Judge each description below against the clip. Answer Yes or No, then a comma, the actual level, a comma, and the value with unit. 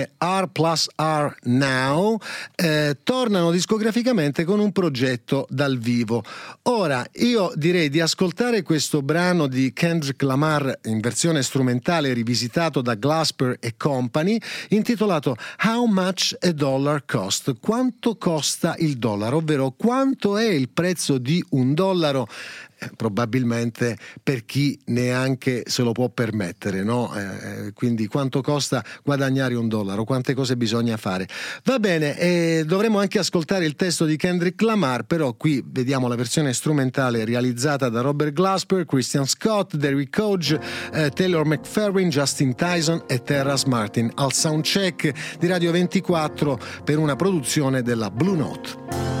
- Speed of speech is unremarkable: Yes, average, 135 wpm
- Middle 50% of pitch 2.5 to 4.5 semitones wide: No, wide, 5.6 semitones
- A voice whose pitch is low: No, medium, 150 Hz